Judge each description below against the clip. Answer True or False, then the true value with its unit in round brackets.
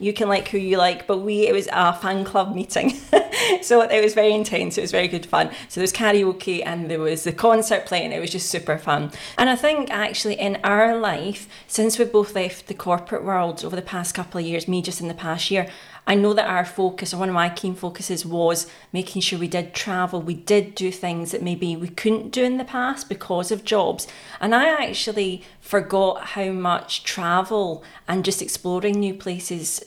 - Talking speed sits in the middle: False (220 wpm)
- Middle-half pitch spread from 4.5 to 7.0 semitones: False (2.9 semitones)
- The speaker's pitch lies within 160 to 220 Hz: True (190 Hz)